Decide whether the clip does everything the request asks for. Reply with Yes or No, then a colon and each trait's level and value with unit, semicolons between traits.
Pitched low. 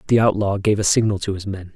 Yes: low, 100 Hz